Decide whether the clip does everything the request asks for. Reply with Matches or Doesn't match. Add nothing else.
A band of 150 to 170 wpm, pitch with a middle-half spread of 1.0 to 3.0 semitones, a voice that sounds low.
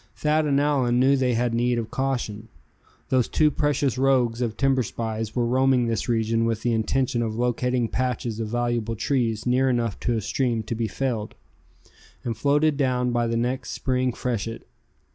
Doesn't match